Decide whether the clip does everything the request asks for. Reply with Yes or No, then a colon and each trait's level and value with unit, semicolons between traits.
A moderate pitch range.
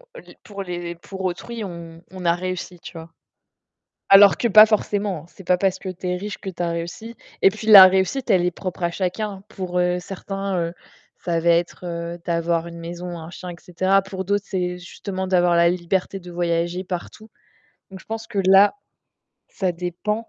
No: narrow, 2.2 semitones